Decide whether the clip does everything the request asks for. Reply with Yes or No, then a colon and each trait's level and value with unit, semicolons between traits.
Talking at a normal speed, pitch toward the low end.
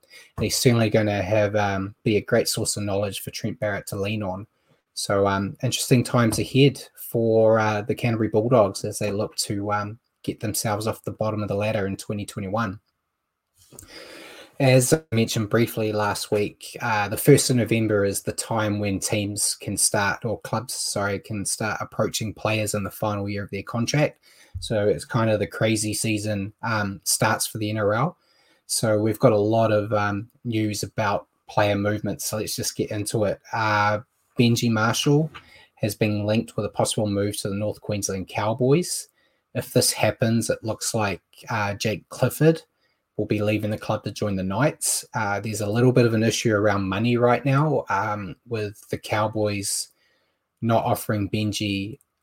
Yes: average, 180 wpm; low, 105 Hz